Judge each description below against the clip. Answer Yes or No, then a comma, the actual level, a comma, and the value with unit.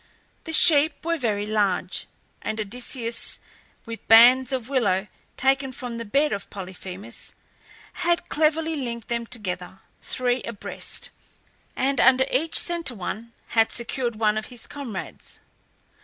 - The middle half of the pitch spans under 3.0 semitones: No, average, 3.9 semitones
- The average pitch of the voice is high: Yes, high, 235 Hz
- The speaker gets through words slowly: Yes, slow, 130 wpm